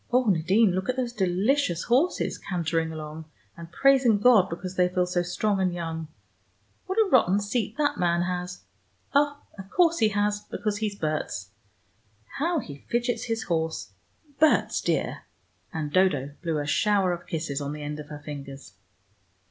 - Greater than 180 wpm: No, average, 170 wpm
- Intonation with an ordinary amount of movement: No, wide, 5.9 semitones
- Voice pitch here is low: No, medium, 185 Hz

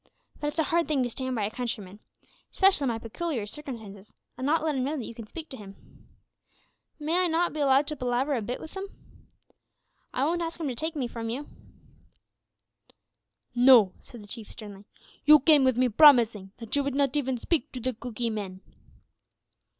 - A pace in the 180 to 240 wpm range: Yes, average, 200 wpm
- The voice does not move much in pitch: No, average, 4.9 semitones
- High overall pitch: Yes, very high, 255 Hz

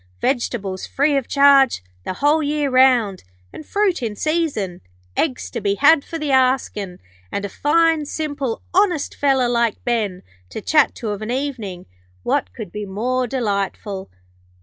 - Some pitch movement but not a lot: No, wide, 5.8 semitones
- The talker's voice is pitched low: No, very high, 255 Hz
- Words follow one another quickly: No, average, 155 wpm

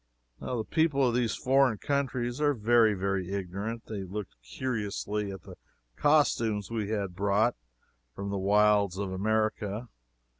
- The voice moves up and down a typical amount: Yes, average, 3.4 semitones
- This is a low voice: Yes, low, 105 Hz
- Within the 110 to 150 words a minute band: Yes, average, 140 wpm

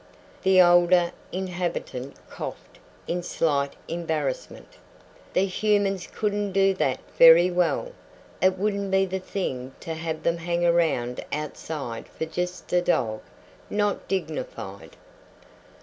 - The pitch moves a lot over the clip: No, average, 3.2 semitones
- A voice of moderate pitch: Yes, medium, 175 Hz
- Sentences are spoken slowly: Yes, slow, 120 wpm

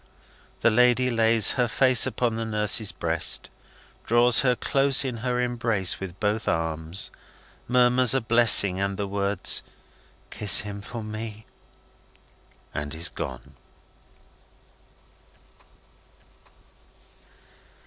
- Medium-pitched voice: No, low, 110 Hz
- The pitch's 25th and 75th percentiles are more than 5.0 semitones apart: No, average, 3.7 semitones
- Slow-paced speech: Yes, slow, 105 wpm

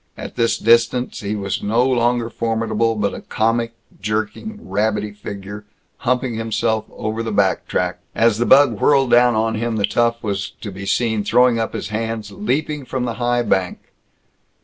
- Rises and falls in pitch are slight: Yes, narrow, 2.2 semitones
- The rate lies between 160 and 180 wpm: Yes, average, 170 wpm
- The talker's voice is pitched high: No, low, 115 Hz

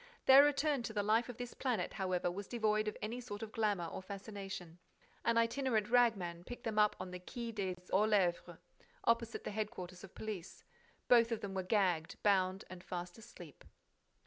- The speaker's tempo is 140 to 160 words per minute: No, average, 185 wpm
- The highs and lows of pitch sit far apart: No, average, 3.9 semitones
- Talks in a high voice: Yes, high, 210 Hz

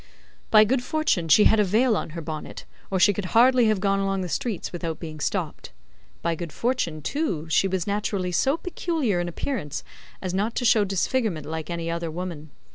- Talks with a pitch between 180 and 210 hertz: Yes, high, 190 Hz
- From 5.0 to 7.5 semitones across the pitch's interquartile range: Yes, average, 5.3 semitones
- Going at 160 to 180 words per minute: No, average, 200 wpm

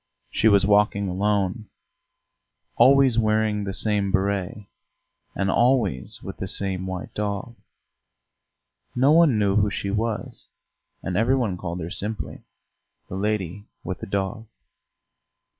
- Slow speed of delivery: Yes, slow, 125 wpm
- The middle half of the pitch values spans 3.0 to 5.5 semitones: No, narrow, 2.4 semitones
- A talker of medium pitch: No, low, 105 Hz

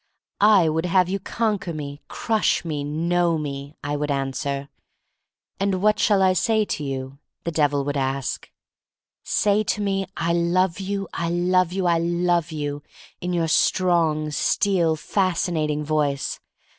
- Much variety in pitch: No, average, 4.0 semitones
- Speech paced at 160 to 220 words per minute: No, average, 150 wpm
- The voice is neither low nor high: Yes, medium, 170 Hz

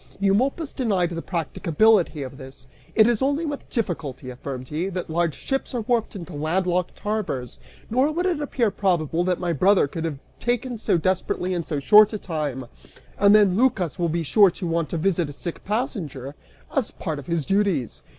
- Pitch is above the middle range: No, medium, 180 Hz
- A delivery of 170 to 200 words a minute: Yes, average, 190 wpm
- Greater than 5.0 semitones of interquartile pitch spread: Yes, wide, 5.4 semitones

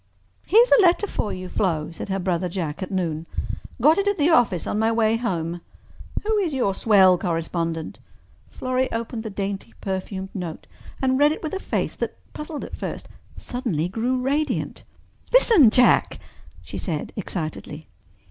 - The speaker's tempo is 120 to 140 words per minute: No, average, 165 wpm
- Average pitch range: No, wide, 6.9 semitones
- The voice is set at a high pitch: Yes, high, 205 Hz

